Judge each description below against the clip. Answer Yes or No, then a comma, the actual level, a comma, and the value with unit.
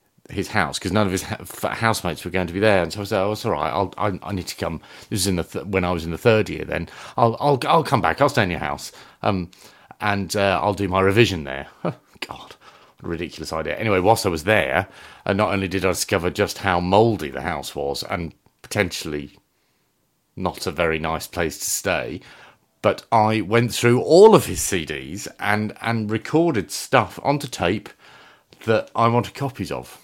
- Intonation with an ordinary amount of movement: Yes, average, 3.9 semitones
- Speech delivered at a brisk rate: Yes, fast, 210 wpm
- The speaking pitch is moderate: No, low, 100 Hz